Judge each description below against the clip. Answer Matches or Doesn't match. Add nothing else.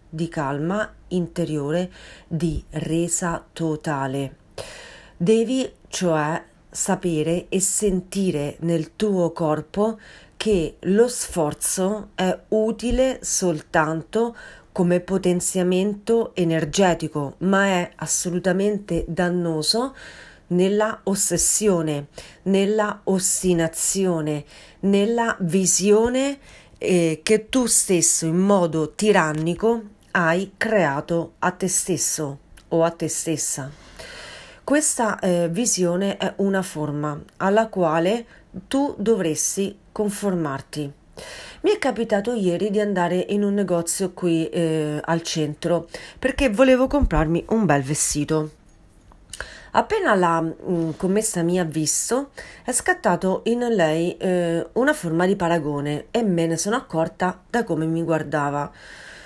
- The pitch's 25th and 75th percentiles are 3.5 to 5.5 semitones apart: Matches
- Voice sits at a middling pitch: Matches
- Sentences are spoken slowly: Matches